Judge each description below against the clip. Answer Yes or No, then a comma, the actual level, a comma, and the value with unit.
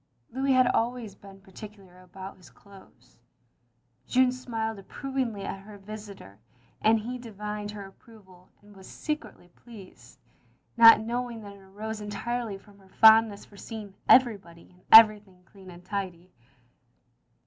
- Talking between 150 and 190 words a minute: No, average, 140 wpm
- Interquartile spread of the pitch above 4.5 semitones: No, average, 2.8 semitones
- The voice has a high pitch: Yes, high, 210 Hz